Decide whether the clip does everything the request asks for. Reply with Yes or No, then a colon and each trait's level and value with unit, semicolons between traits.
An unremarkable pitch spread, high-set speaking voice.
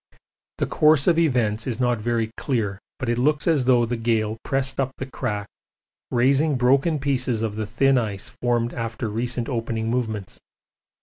No: average, 3.0 semitones; low, 120 Hz